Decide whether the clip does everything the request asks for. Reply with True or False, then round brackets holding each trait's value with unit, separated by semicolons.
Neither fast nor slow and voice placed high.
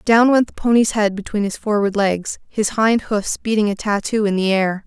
False (220 wpm; 210 Hz)